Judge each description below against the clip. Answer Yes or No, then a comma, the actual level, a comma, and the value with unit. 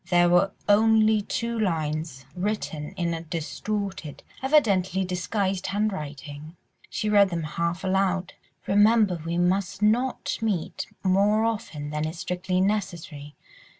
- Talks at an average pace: No, slow, 120 wpm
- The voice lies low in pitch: No, medium, 185 Hz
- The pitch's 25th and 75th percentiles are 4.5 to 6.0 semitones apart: No, average, 3.9 semitones